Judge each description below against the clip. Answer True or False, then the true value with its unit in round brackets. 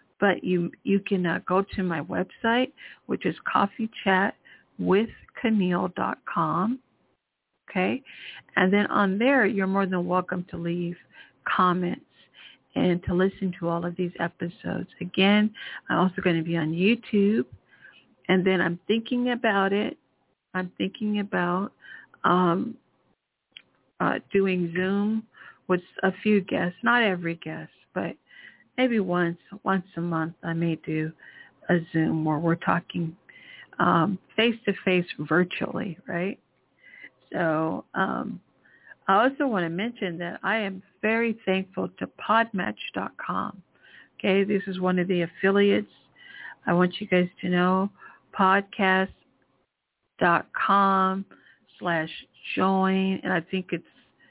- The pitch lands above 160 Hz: True (190 Hz)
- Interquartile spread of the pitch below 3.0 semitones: True (2.5 semitones)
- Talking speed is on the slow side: True (125 wpm)